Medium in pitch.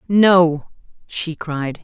Yes: medium, 170 Hz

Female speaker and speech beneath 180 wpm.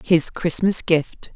Yes: female; slow, 135 wpm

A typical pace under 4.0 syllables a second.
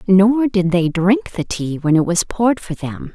No: 4.4 syllables/s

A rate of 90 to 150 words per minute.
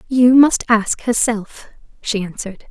Yes: slow, 135 wpm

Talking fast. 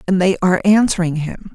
No: average, 195 wpm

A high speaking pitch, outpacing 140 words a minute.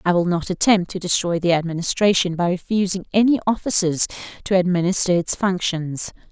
No: medium, 180 Hz; average, 150 wpm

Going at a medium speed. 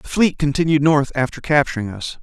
Yes: average, 190 wpm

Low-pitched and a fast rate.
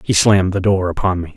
Yes: very low, 95 Hz; fast, 265 wpm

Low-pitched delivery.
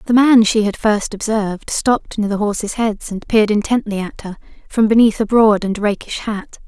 No: high, 215 Hz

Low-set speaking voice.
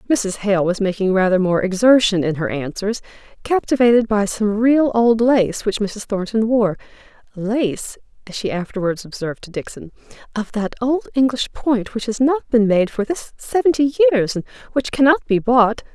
No: high, 220 Hz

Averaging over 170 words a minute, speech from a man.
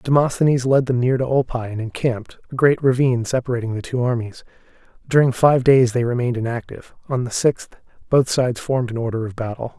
Yes: average, 190 wpm; male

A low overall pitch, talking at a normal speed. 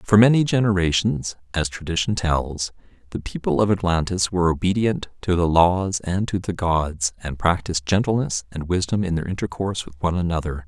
Yes: very low, 90 Hz; average, 170 wpm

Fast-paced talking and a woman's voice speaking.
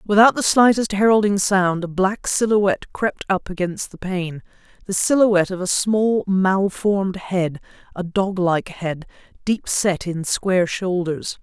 No: average, 145 wpm; female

